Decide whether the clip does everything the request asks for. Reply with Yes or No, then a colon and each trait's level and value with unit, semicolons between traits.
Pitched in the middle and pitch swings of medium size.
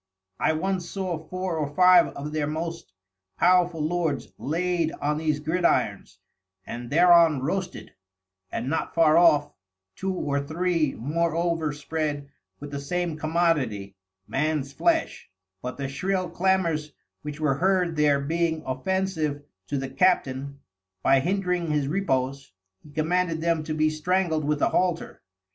Yes: medium, 160 Hz; average, 3.5 semitones